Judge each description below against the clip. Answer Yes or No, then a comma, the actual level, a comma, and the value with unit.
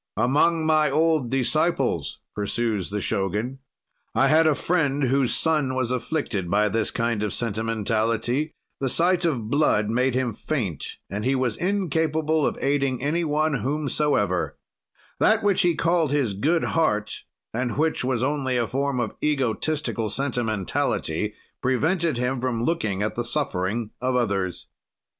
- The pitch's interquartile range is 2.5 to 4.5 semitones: No, average, 5.3 semitones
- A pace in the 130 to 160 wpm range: Yes, average, 145 wpm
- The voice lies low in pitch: Yes, low, 130 Hz